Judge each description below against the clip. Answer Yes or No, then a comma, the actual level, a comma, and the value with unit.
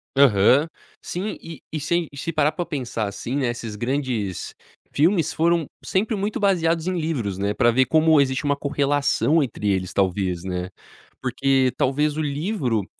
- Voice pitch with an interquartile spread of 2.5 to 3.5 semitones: No, wide, 5.6 semitones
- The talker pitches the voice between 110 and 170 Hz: Yes, medium, 140 Hz